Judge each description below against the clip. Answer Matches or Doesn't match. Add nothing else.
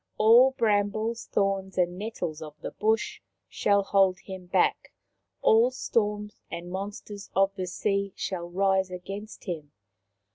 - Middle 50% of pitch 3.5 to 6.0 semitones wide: Doesn't match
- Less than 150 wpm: Matches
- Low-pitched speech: Doesn't match